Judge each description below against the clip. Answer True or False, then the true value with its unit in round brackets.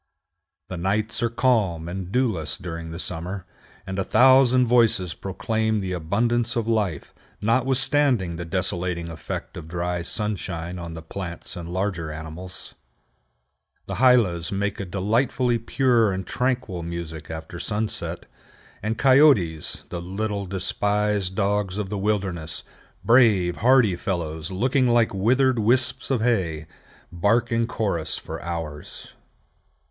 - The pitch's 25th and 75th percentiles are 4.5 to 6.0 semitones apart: True (5.2 semitones)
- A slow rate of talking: True (130 wpm)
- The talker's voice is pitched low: True (100 Hz)